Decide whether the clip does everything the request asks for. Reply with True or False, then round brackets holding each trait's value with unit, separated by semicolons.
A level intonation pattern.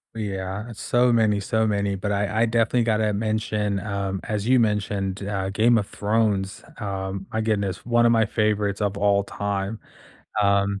True (1.8 semitones)